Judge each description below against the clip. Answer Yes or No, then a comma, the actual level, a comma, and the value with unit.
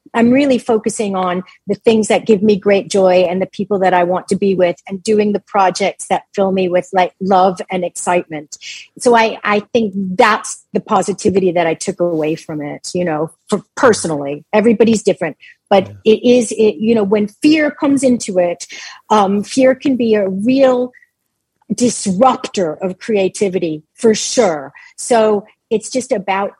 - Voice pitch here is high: Yes, high, 205 Hz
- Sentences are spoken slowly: No, average, 175 wpm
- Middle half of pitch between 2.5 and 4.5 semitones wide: Yes, average, 3.5 semitones